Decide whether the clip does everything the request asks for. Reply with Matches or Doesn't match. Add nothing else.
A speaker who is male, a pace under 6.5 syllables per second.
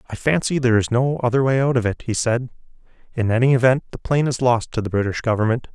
Doesn't match